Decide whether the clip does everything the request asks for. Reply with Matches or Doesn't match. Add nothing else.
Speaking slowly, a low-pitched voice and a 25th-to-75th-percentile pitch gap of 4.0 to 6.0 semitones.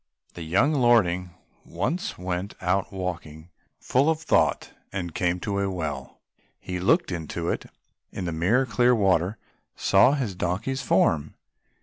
Doesn't match